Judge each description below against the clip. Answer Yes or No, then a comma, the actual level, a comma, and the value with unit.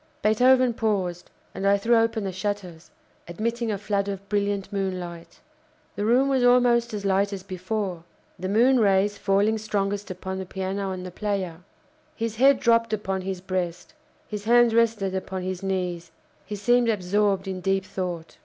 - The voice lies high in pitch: Yes, high, 200 Hz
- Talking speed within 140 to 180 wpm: Yes, average, 165 wpm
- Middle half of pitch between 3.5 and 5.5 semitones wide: No, average, 2.9 semitones